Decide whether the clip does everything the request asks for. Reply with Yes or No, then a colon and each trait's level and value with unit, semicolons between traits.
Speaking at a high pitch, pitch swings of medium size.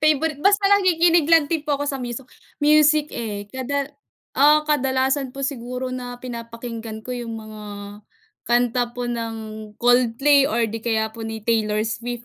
Yes: very high, 250 Hz; average, 4.0 semitones